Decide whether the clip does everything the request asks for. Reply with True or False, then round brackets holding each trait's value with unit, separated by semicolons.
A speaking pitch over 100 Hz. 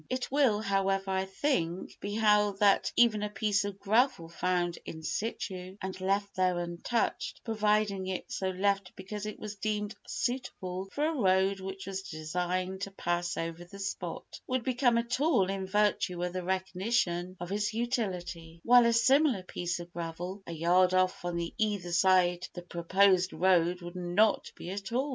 True (190 Hz)